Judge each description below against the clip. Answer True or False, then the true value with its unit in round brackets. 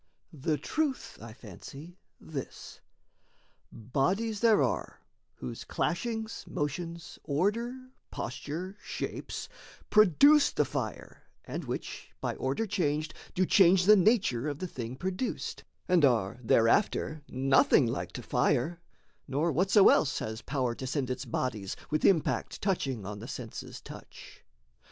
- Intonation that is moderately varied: False (7.0 semitones)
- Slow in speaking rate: True (130 wpm)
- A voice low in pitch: False (150 Hz)